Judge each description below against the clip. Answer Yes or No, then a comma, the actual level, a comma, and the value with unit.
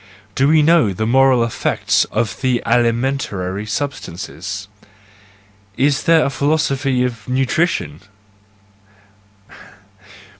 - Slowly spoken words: Yes, slow, 90 wpm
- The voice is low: Yes, low, 130 Hz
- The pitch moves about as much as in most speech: Yes, average, 4.5 semitones